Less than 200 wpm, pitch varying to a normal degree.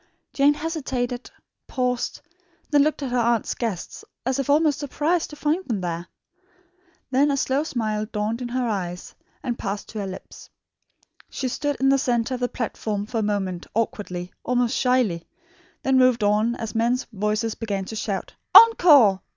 Yes: average, 165 wpm; average, 4.2 semitones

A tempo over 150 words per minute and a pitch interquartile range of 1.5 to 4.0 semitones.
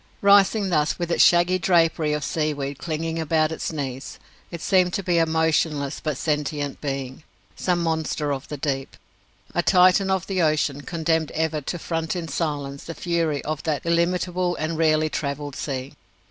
Yes: average, 170 wpm; average, 2.8 semitones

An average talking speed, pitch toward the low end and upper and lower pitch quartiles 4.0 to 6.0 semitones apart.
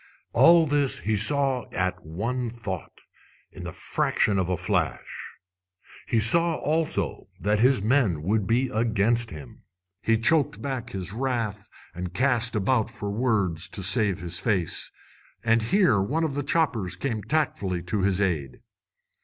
Yes: average, 150 wpm; low, 110 Hz; wide, 5.4 semitones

